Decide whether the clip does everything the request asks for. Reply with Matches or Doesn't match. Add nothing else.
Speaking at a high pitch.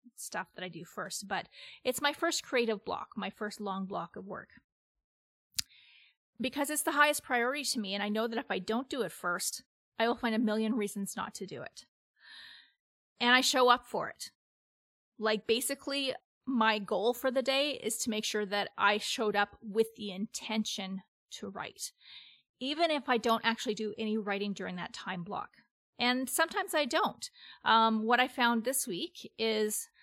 Matches